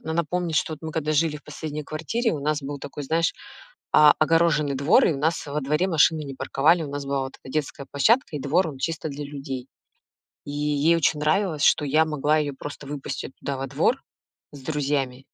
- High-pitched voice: No, medium, 150 Hz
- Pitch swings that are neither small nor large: No, narrow, 2.2 semitones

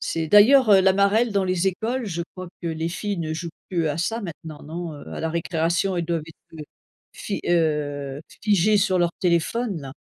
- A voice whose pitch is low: No, medium, 175 Hz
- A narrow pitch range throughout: No, average, 3.7 semitones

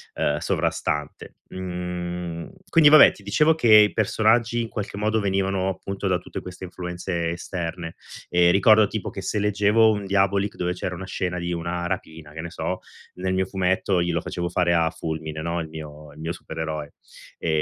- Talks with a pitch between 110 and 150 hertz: No, very low, 90 Hz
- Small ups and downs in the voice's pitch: No, average, 3.0 semitones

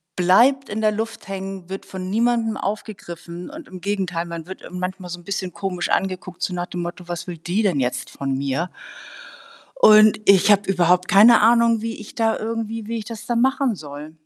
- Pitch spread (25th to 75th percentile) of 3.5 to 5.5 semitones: Yes, average, 3.9 semitones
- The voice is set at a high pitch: Yes, high, 195 Hz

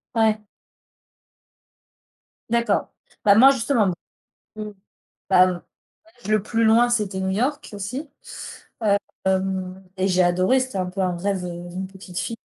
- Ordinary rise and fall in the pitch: Yes, average, 3.5 semitones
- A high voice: Yes, high, 195 Hz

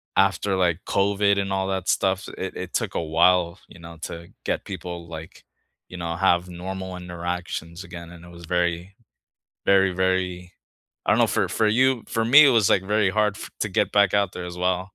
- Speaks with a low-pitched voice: Yes, very low, 90 Hz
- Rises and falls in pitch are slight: Yes, narrow, 2.2 semitones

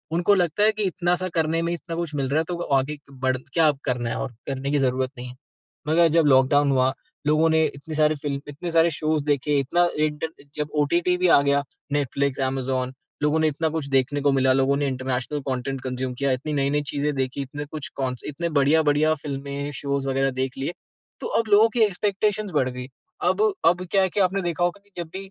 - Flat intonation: No, average, 3.7 semitones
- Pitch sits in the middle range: Yes, medium, 145 Hz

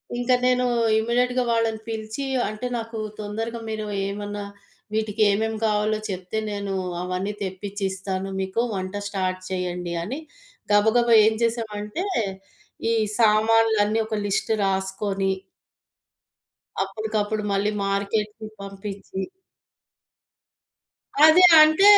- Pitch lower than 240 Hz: Yes, high, 210 Hz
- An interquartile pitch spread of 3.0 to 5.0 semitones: No, narrow, 2.4 semitones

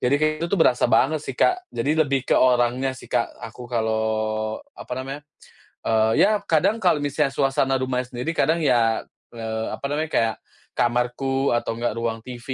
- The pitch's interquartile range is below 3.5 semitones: No, average, 3.8 semitones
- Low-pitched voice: Yes, low, 130 Hz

